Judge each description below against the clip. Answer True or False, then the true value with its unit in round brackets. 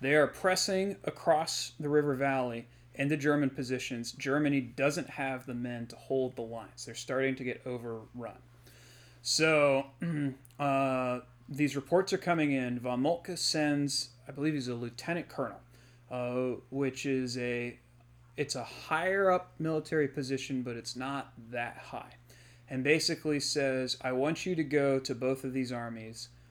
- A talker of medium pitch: False (130 Hz)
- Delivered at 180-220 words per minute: False (155 wpm)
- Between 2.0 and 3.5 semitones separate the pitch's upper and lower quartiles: True (3.1 semitones)